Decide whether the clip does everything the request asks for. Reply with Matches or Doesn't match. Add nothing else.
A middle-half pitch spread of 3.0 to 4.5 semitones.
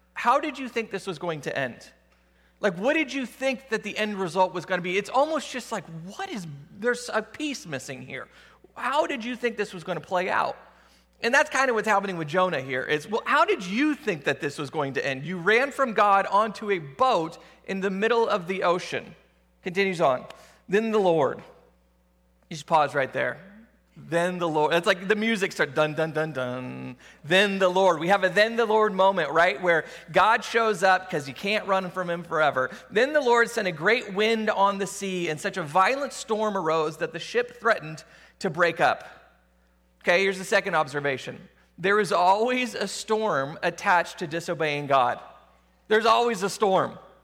Doesn't match